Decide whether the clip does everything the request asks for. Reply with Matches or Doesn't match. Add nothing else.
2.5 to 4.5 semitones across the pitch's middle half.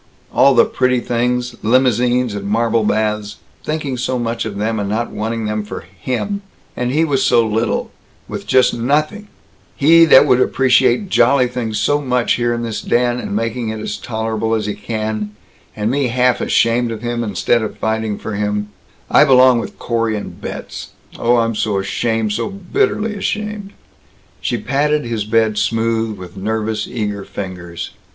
Matches